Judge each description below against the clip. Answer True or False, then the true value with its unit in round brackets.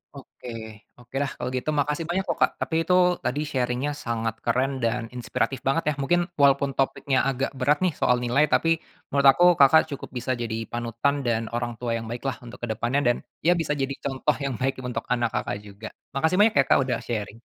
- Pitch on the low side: True (130 Hz)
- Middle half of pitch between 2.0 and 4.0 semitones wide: True (3.0 semitones)